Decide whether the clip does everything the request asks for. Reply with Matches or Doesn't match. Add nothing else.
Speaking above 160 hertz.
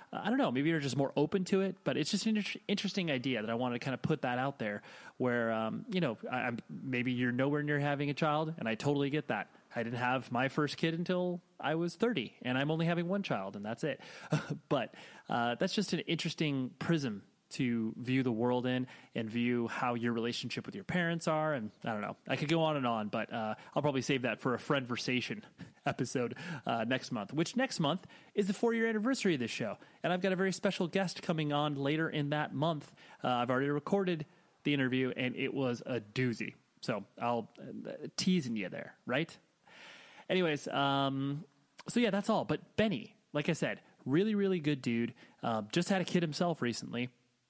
Doesn't match